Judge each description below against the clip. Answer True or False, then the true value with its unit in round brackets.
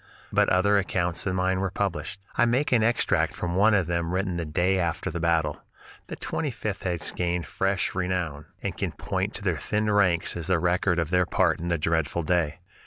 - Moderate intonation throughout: False (2.3 semitones)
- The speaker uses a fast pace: True (210 wpm)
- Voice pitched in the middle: False (90 Hz)